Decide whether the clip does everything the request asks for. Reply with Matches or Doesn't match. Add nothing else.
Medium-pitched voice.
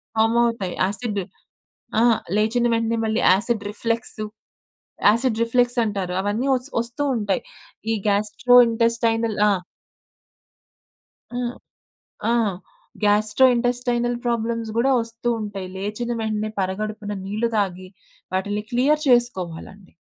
Doesn't match